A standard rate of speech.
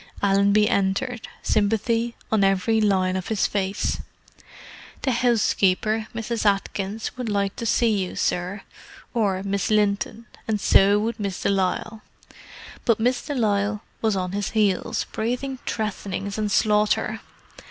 No: slow, 125 wpm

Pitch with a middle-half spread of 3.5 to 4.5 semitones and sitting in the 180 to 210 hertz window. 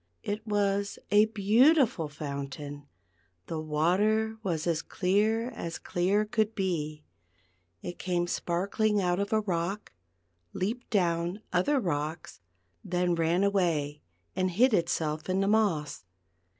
Yes: average, 4.2 semitones; medium, 185 Hz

